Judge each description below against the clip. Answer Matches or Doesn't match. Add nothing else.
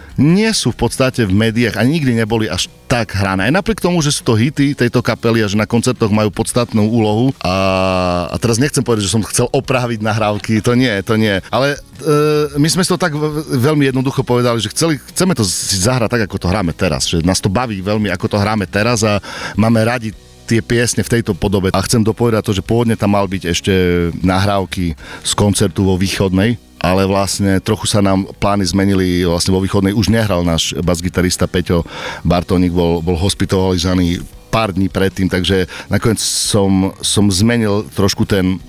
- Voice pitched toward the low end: Matches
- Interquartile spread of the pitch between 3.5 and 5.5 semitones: Matches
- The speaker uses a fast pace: Matches